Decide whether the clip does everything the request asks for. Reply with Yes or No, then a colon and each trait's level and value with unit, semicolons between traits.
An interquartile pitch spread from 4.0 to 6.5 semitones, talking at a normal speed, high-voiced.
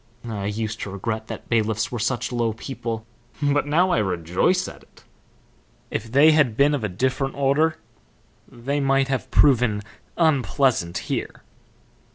No: average, 4.4 semitones; average, 150 wpm; low, 125 Hz